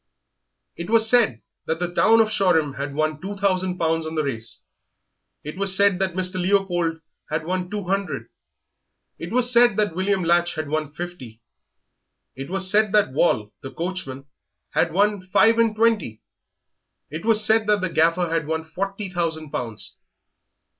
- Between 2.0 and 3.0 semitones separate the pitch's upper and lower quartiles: No, average, 4.1 semitones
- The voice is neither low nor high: Yes, medium, 180 Hz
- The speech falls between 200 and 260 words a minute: No, average, 165 wpm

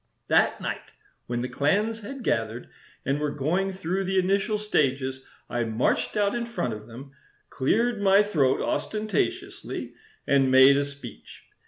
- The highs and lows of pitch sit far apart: Yes, wide, 7.6 semitones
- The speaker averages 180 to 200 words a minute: No, average, 150 wpm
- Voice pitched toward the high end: No, medium, 150 Hz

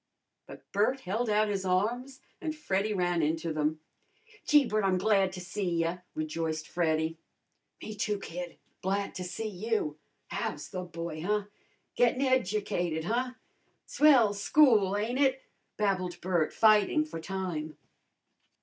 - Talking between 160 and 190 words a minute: No, average, 140 wpm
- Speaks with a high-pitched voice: Yes, high, 195 Hz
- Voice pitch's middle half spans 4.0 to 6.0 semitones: Yes, average, 4.3 semitones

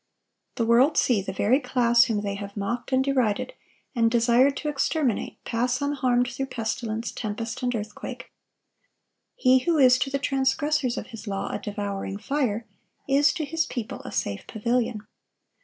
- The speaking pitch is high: Yes, high, 245 Hz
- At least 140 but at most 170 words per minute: Yes, average, 160 wpm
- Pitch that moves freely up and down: No, average, 3.6 semitones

